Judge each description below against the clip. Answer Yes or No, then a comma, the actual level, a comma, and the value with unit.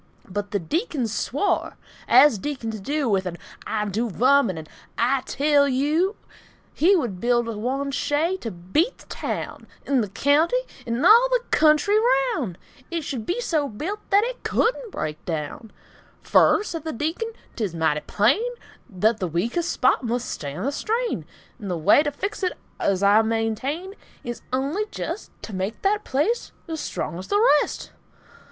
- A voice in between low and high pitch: No, very high, 270 Hz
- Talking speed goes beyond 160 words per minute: Yes, average, 170 wpm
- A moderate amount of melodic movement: No, wide, 8.3 semitones